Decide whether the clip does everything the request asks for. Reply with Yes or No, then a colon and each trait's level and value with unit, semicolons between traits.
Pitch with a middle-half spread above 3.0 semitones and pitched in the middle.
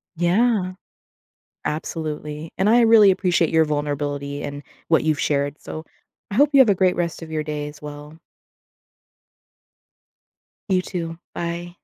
Yes: average, 3.7 semitones; medium, 165 Hz